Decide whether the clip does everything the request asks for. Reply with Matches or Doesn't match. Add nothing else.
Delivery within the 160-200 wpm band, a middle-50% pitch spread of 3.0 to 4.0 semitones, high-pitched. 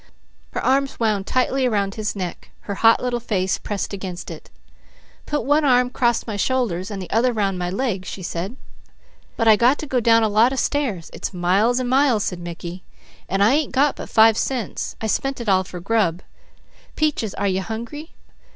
Doesn't match